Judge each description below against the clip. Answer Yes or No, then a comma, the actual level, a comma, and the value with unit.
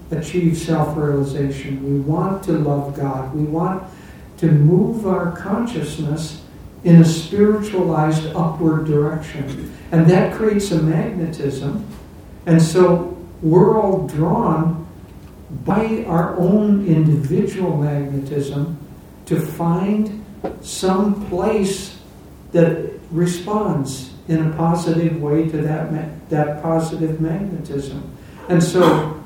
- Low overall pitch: No, medium, 165 Hz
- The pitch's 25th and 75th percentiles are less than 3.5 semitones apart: Yes, average, 3.1 semitones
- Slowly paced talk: Yes, slow, 105 wpm